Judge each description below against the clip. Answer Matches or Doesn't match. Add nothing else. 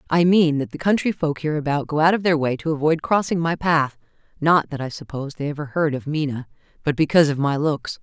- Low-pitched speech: Doesn't match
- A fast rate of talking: Matches